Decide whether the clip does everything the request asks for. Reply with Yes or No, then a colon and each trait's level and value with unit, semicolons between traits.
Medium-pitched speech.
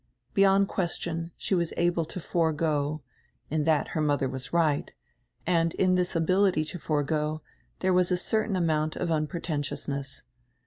Yes: medium, 165 Hz